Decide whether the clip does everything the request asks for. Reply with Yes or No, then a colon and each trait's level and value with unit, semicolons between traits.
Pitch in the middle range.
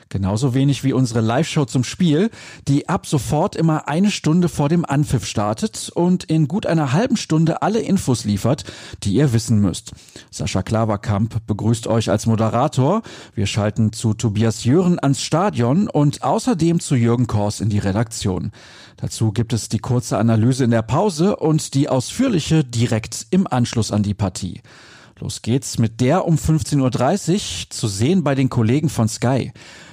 No: low, 130 Hz